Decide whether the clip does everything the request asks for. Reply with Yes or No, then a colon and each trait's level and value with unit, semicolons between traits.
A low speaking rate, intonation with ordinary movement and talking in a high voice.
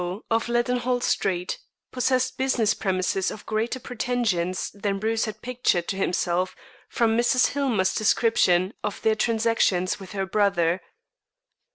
Yes: slow, 130 wpm; average, 4.2 semitones; high, 215 Hz